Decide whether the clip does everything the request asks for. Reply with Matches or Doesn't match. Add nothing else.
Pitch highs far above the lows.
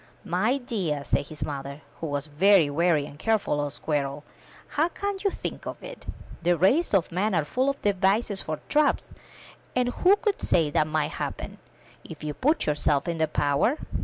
Matches